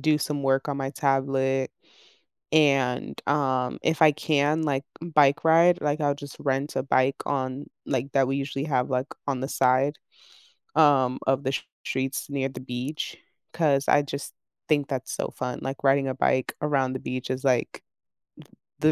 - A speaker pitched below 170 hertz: Yes, low, 135 Hz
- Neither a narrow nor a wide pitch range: No, narrow, 1.8 semitones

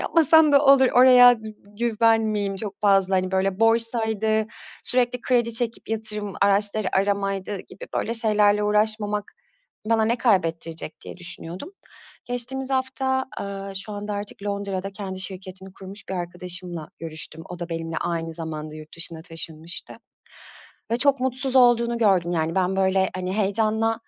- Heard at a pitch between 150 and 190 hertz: No, high, 205 Hz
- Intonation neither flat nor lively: Yes, average, 3.7 semitones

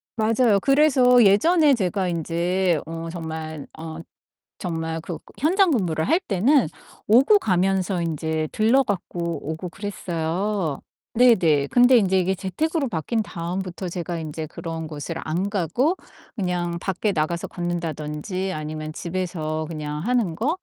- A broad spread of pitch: No, average, 5.0 semitones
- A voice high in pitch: No, medium, 180 Hz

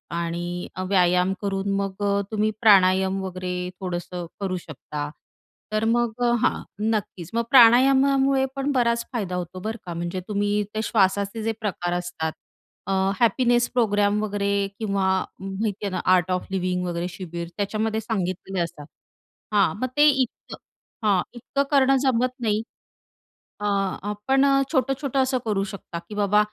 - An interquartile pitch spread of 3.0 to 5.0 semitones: Yes, average, 4.2 semitones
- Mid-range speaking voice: No, high, 205 Hz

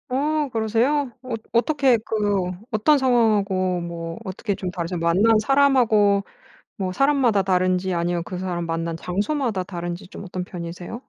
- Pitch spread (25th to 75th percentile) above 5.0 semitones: Yes, wide, 5.4 semitones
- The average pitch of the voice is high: Yes, high, 200 Hz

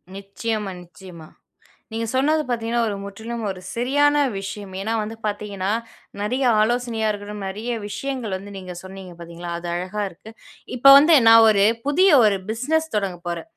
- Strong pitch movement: No, average, 3.7 semitones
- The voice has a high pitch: Yes, high, 210 Hz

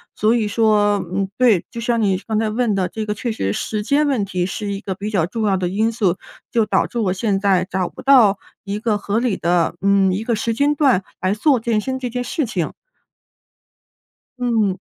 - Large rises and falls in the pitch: No, average, 3.2 semitones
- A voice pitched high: Yes, high, 210 Hz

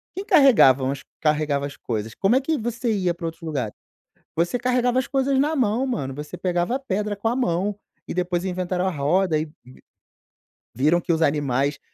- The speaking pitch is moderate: Yes, medium, 180 Hz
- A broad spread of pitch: Yes, wide, 8.1 semitones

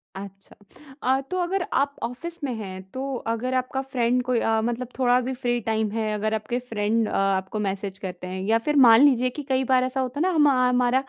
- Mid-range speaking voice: No, high, 245 Hz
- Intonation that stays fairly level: No, average, 3.4 semitones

